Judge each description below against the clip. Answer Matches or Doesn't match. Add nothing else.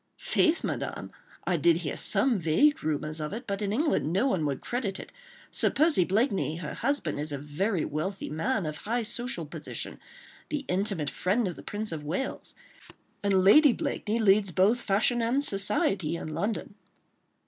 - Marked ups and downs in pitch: Matches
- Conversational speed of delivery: Matches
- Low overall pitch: Doesn't match